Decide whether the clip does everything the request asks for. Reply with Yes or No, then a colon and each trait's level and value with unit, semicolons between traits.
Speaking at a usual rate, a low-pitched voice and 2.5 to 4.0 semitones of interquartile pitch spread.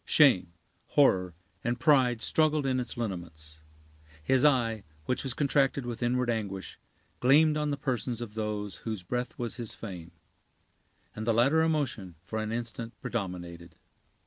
No: average, 145 wpm; low, 120 Hz; average, 4.8 semitones